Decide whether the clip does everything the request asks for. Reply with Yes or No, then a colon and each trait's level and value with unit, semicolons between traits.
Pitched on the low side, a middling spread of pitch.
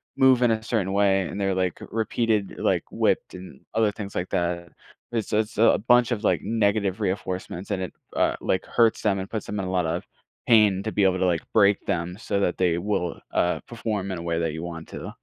Yes: low, 100 Hz; average, 3.3 semitones